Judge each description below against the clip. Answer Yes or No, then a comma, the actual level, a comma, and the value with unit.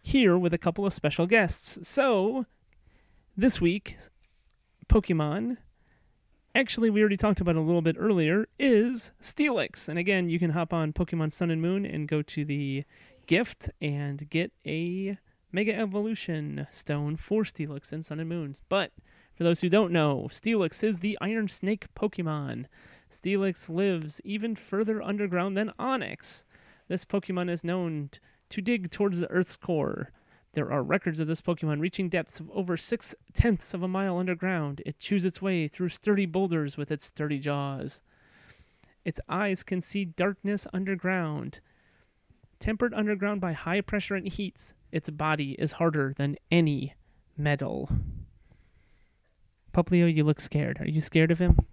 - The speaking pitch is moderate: Yes, medium, 175 Hz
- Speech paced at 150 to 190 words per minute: Yes, average, 160 wpm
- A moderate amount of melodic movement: Yes, average, 4.4 semitones